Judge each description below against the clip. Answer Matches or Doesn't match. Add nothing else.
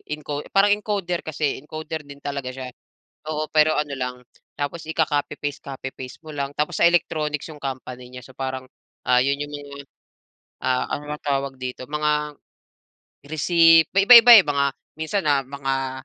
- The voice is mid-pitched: Matches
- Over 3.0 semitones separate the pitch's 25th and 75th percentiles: Doesn't match